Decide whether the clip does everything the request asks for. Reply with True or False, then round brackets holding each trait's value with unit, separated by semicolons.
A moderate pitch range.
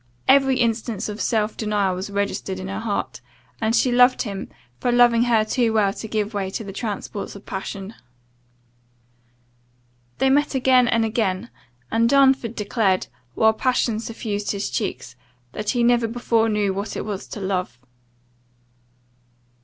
True (3.1 semitones)